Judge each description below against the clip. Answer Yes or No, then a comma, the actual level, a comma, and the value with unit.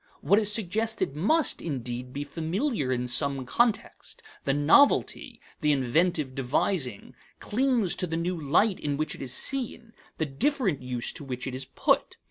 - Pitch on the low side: No, medium, 160 Hz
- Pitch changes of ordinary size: No, wide, 8.0 semitones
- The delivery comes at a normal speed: Yes, average, 160 wpm